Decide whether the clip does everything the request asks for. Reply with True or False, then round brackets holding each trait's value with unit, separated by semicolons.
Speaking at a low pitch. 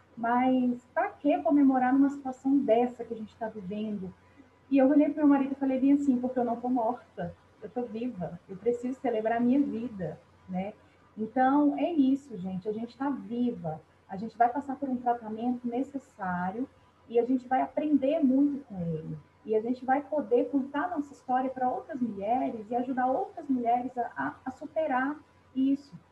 False (250 Hz)